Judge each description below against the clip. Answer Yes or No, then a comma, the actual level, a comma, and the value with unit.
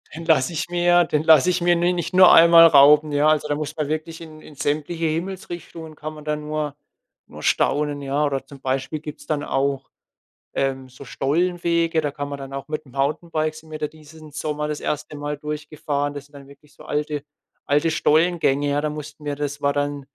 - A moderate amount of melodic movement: No, narrow, 1.8 semitones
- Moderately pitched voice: Yes, medium, 150 Hz